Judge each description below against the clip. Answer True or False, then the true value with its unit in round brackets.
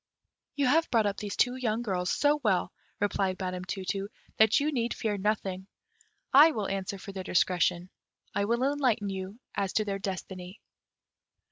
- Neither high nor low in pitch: False (200 Hz)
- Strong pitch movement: False (3.8 semitones)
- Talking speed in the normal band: True (170 wpm)